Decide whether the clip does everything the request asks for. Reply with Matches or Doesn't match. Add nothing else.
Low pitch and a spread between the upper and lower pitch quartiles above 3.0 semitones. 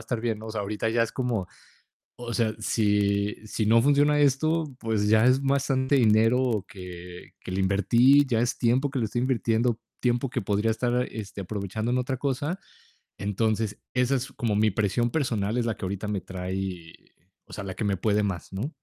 Matches